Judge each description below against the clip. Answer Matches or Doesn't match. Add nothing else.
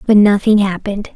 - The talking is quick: Doesn't match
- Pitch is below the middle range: Doesn't match